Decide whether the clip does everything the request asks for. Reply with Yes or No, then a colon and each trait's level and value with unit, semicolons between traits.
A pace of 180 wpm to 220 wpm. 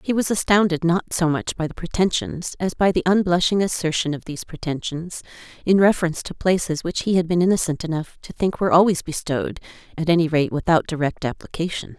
Yes: average, 190 wpm